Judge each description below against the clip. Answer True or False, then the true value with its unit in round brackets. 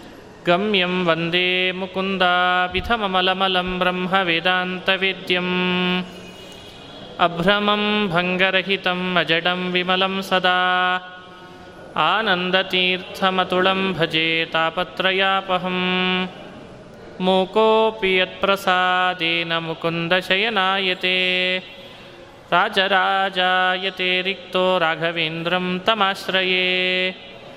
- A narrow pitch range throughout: True (0.9 semitones)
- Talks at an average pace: False (45 wpm)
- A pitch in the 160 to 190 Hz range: True (185 Hz)